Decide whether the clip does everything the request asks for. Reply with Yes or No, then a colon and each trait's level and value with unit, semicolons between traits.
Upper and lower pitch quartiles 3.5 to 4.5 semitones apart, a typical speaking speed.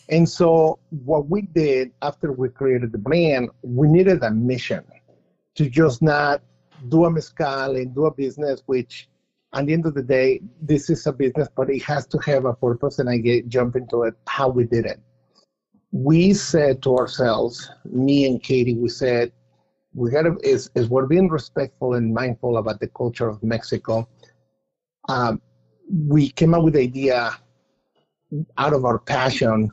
Yes: average, 4.1 semitones; average, 175 wpm